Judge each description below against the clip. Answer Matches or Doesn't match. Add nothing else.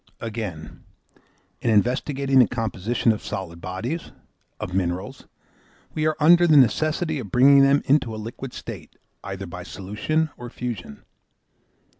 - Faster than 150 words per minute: Doesn't match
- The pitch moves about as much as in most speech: Doesn't match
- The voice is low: Matches